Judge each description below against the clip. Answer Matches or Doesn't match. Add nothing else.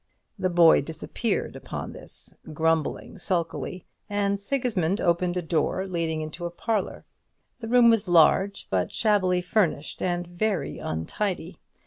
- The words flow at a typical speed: Doesn't match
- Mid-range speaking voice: Matches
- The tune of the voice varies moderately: Matches